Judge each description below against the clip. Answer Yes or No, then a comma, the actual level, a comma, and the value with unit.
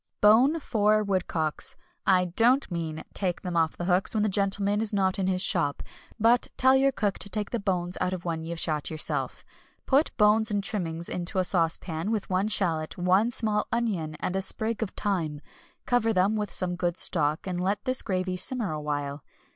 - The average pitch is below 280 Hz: Yes, high, 190 Hz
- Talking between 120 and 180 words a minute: No, average, 195 wpm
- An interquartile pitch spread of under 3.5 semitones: No, average, 3.9 semitones